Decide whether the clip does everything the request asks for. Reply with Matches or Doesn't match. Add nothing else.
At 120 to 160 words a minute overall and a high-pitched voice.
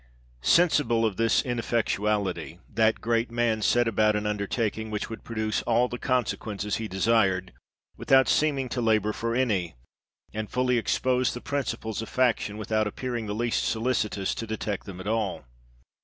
Doesn't match